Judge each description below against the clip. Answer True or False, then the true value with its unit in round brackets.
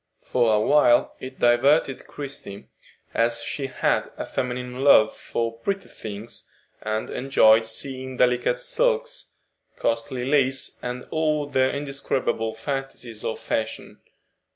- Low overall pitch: True (125 Hz)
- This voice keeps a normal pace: False (120 wpm)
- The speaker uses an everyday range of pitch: True (3.2 semitones)